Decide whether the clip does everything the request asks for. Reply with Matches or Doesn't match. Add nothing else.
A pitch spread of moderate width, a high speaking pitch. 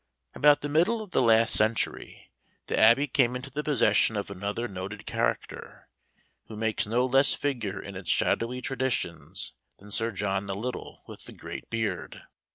Doesn't match